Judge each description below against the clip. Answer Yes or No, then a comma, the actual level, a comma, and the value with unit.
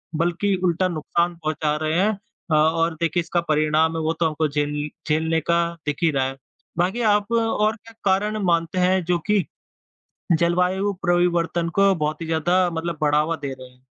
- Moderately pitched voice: Yes, medium, 170 Hz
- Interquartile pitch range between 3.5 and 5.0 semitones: No, average, 2.7 semitones